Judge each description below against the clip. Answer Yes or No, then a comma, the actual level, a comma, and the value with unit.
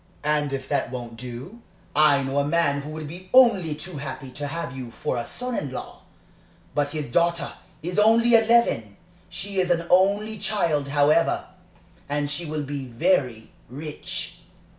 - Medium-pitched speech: Yes, medium, 150 Hz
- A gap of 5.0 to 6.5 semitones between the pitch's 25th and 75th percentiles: No, average, 4.6 semitones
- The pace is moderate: Yes, average, 165 wpm